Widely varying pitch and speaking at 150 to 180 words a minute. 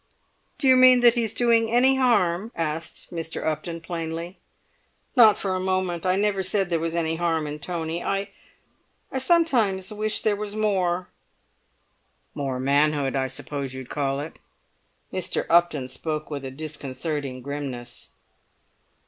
No: wide, 5.9 semitones; average, 140 wpm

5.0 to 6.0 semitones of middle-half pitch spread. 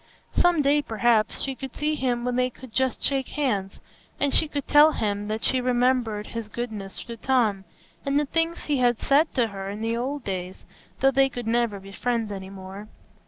No: average, 4.3 semitones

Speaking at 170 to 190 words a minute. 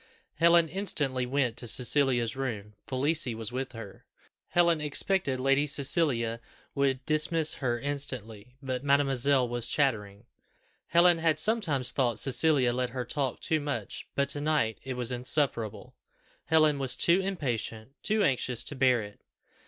No: average, 145 wpm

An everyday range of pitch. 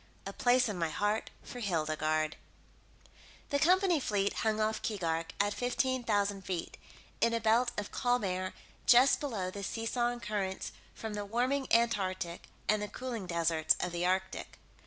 Yes: average, 4.5 semitones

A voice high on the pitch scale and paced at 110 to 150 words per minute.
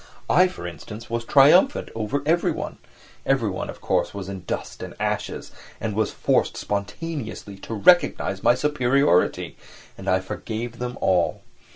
No: low, 115 Hz; average, 145 wpm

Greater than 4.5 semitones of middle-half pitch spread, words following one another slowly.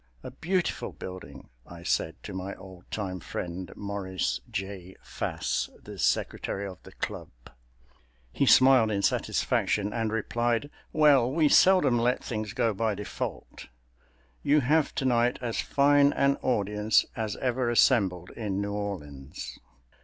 Yes: average, 5.2 semitones; slow, 130 wpm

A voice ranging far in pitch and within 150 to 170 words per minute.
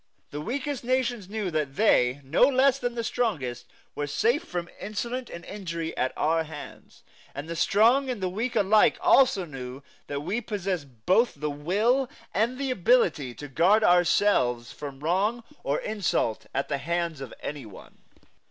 Yes: wide, 8.2 semitones; average, 165 wpm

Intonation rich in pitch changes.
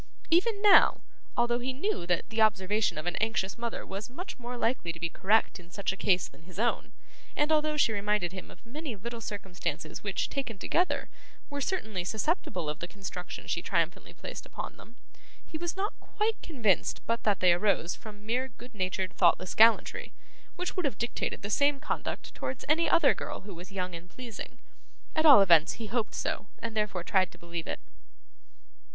Yes: wide, 6.0 semitones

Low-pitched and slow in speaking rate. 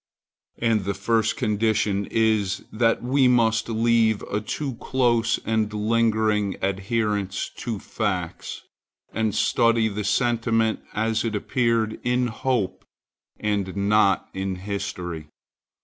Yes: low, 110 Hz; slow, 115 wpm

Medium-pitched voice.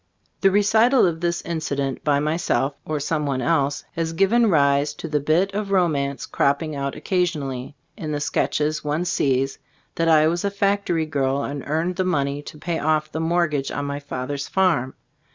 Yes: medium, 155 Hz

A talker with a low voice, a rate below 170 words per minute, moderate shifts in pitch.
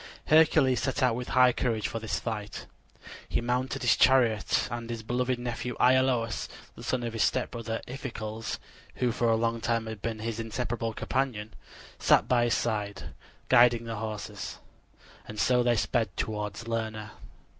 No: low, 115 Hz; average, 160 wpm; narrow, 1.9 semitones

